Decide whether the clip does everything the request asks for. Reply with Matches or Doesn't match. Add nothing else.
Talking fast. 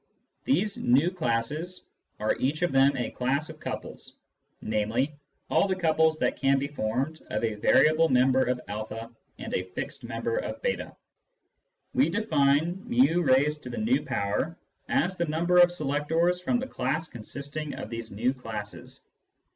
Doesn't match